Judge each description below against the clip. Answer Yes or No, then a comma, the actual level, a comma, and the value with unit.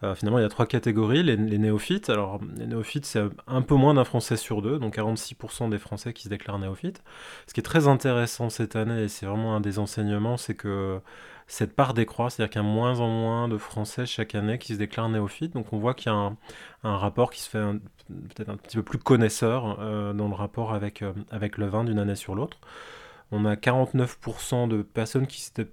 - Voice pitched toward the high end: No, low, 110 Hz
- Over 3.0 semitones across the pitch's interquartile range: No, average, 2.7 semitones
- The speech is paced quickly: Yes, fast, 235 wpm